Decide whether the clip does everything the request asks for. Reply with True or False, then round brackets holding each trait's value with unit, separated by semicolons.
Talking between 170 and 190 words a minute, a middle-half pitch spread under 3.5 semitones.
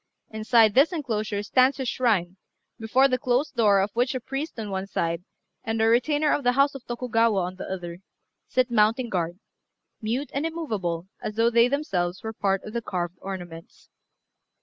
False (180 wpm; 4.8 semitones)